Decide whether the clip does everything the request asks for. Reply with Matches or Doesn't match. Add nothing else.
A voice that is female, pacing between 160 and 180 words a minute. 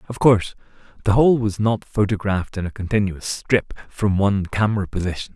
Doesn't match